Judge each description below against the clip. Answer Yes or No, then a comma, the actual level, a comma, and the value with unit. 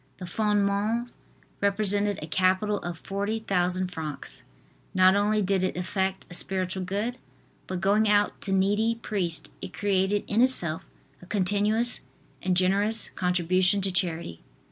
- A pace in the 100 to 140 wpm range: Yes, slow, 135 wpm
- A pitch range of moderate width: No, narrow, 2.2 semitones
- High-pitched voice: Yes, high, 195 Hz